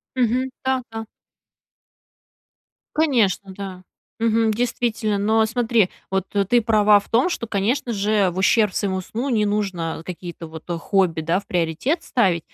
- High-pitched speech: Yes, high, 210 Hz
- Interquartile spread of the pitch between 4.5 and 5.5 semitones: No, average, 3.6 semitones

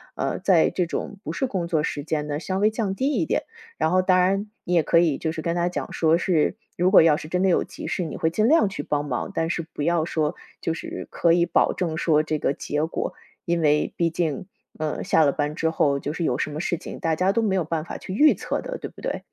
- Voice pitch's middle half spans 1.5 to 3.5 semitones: Yes, average, 3.0 semitones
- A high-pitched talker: No, medium, 170 Hz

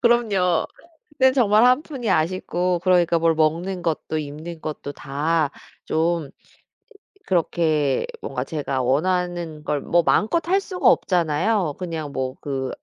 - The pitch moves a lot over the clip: No, average, 3.6 semitones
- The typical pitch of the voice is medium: Yes, medium, 170 Hz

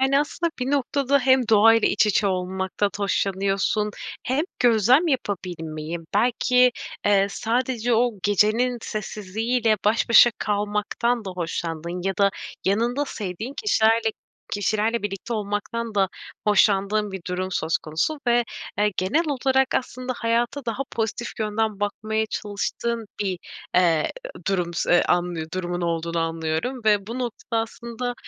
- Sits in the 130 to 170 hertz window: No, high, 215 Hz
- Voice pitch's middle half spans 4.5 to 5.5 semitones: No, average, 3.9 semitones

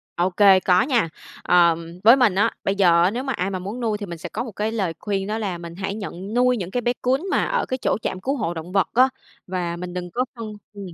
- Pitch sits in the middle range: No, high, 200 Hz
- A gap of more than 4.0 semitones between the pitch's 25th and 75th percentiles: Yes, average, 4.4 semitones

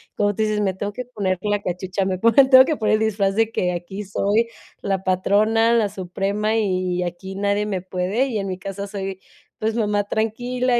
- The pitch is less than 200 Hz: No, high, 205 Hz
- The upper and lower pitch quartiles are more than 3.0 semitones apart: No, narrow, 2.6 semitones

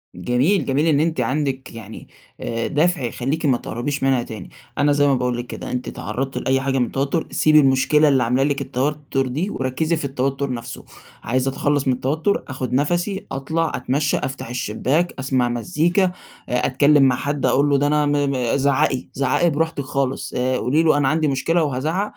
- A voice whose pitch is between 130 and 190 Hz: Yes, low, 135 Hz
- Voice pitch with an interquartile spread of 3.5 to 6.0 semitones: No, average, 2.7 semitones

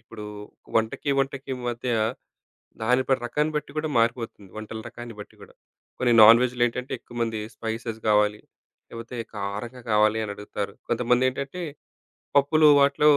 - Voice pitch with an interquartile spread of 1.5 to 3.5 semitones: Yes, average, 2.9 semitones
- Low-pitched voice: Yes, low, 120 Hz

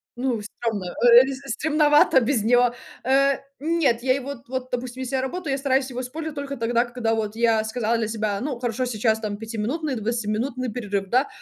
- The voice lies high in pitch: Yes, high, 245 Hz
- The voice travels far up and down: No, average, 3.1 semitones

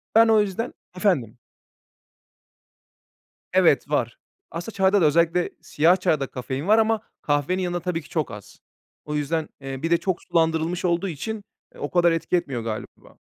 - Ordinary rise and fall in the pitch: Yes, average, 4.0 semitones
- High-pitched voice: No, medium, 170 Hz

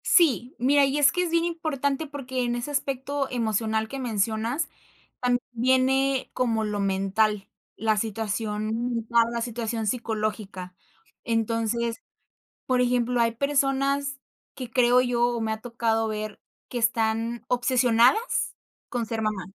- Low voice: No, high, 235 Hz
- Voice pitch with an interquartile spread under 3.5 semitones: Yes, average, 3.0 semitones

